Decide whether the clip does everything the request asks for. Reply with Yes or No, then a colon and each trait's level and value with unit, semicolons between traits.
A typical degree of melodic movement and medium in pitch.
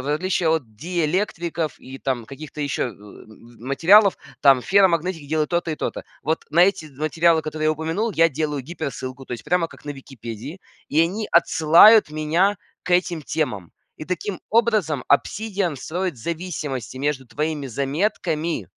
Yes: average, 4.2 semitones; medium, 155 Hz